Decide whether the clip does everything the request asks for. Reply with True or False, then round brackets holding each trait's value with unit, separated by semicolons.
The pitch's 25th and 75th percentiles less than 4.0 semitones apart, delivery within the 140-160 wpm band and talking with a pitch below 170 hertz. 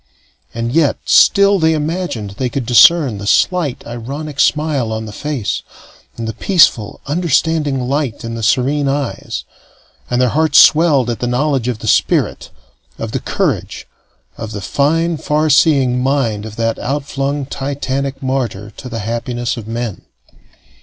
False (4.3 semitones; 155 wpm; 135 Hz)